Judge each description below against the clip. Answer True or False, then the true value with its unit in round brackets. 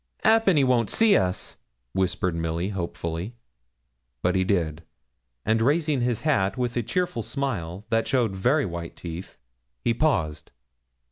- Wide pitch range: True (6.8 semitones)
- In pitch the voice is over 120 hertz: False (110 Hz)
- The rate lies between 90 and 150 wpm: True (140 wpm)